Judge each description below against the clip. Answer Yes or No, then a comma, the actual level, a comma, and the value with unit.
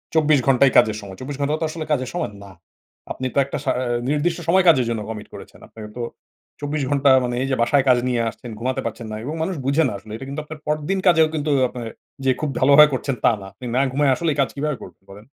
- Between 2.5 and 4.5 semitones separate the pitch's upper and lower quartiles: Yes, average, 3.6 semitones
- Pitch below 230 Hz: Yes, medium, 140 Hz